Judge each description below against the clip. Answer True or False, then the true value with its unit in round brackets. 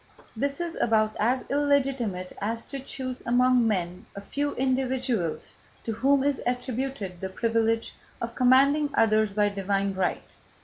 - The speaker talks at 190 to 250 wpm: False (140 wpm)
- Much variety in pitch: False (4.3 semitones)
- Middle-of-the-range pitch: False (235 Hz)